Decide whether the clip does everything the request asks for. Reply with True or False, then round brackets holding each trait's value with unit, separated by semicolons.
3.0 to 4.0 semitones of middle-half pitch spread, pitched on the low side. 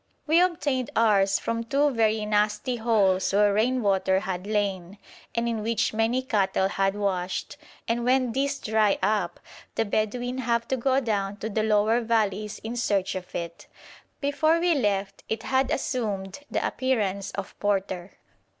False (3.6 semitones; 215 Hz)